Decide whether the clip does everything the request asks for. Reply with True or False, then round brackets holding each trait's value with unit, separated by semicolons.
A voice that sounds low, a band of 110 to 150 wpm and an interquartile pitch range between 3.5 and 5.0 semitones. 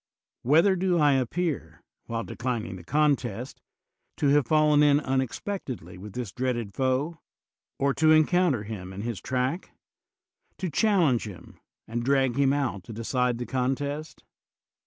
True (130 Hz; 140 wpm; 4.4 semitones)